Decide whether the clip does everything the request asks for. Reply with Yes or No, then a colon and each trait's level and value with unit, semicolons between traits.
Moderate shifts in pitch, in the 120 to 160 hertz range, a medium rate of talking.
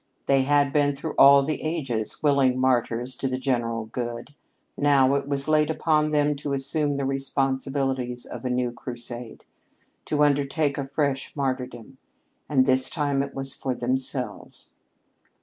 No: narrow, 2.0 semitones; low, 135 Hz; average, 150 wpm